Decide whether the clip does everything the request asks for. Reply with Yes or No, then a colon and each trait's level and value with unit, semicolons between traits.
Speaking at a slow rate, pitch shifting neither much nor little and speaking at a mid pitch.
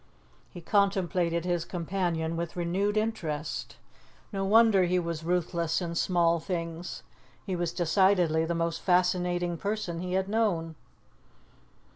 No: slow, 125 wpm; narrow, 2.2 semitones; medium, 175 Hz